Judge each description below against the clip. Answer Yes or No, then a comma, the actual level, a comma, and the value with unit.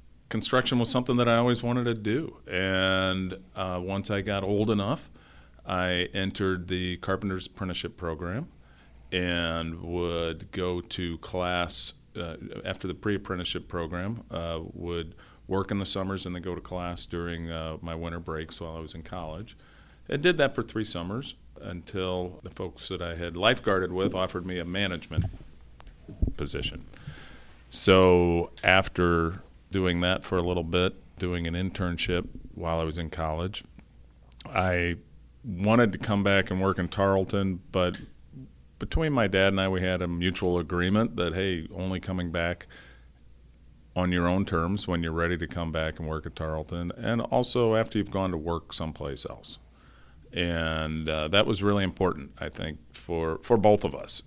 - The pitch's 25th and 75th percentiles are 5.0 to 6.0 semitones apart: No, average, 2.8 semitones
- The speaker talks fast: No, average, 165 wpm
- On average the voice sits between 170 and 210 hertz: No, very low, 90 Hz